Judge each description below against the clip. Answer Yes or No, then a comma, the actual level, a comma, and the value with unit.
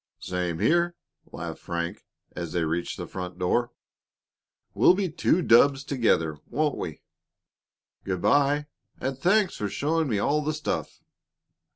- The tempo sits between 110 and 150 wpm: Yes, average, 140 wpm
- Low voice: Yes, low, 130 Hz